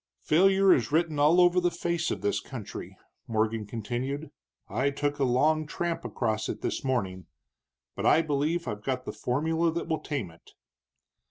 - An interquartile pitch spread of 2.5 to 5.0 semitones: No, wide, 5.6 semitones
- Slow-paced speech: No, average, 170 wpm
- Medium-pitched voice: Yes, medium, 145 Hz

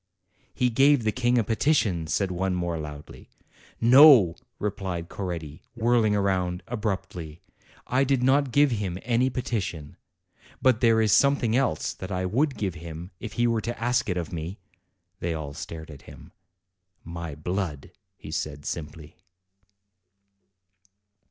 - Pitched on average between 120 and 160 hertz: No, low, 100 Hz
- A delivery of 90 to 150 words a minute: Yes, average, 145 wpm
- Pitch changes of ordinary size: No, wide, 6.1 semitones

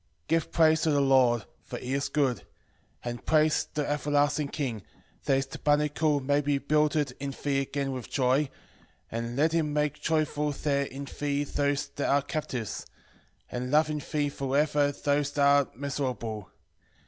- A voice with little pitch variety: Yes, narrow, 1.8 semitones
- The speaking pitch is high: No, medium, 145 Hz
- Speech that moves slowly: No, average, 170 wpm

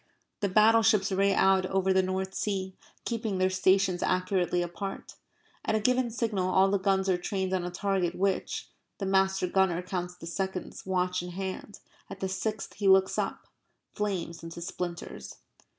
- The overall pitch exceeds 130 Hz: Yes, high, 190 Hz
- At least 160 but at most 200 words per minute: Yes, average, 165 wpm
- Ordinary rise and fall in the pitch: No, narrow, 1.3 semitones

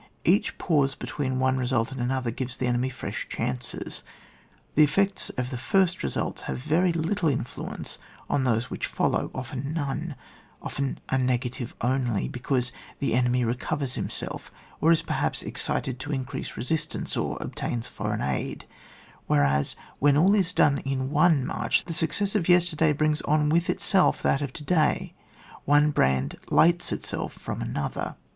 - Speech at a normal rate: Yes, average, 160 wpm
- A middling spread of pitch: Yes, average, 4.2 semitones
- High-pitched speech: No, low, 135 Hz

